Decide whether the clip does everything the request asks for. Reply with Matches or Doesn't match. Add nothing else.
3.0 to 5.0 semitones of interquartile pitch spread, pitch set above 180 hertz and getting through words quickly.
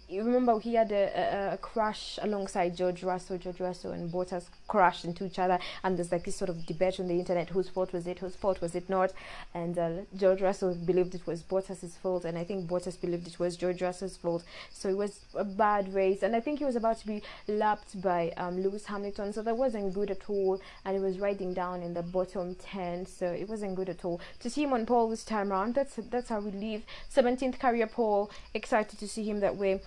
Doesn't match